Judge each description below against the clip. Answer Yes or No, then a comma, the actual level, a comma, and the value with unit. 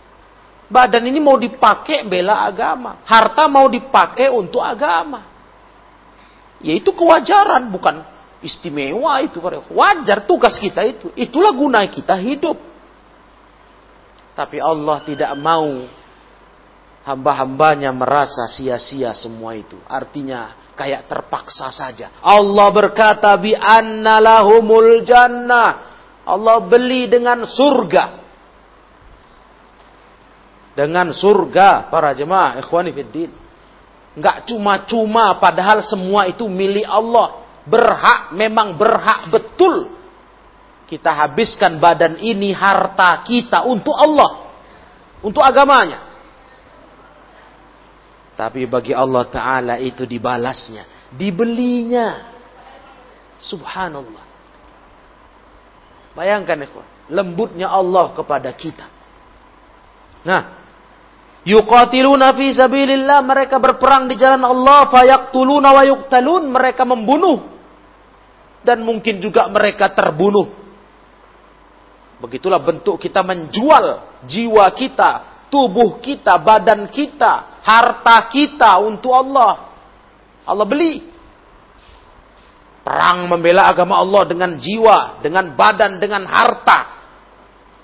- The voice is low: No, high, 215 Hz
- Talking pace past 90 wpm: No, slow, 85 wpm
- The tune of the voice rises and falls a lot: Yes, wide, 7.1 semitones